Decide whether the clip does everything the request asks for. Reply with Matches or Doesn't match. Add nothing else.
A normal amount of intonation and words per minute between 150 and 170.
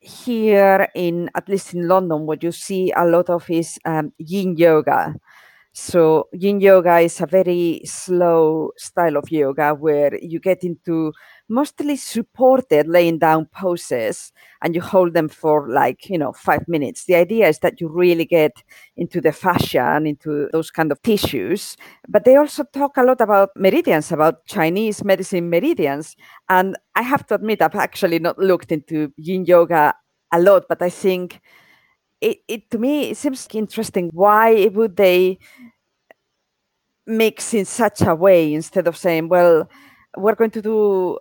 Matches